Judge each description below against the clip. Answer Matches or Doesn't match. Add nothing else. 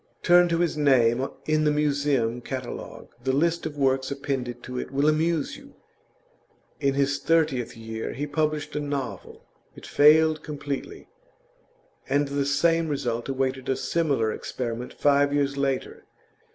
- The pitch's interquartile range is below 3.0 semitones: Matches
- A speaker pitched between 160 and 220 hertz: Doesn't match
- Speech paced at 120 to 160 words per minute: Matches